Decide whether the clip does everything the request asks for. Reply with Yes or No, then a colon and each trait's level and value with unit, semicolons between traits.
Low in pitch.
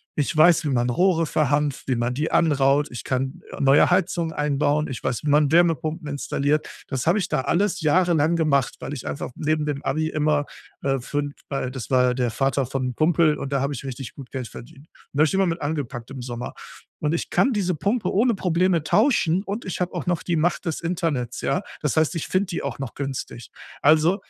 No: medium, 150 Hz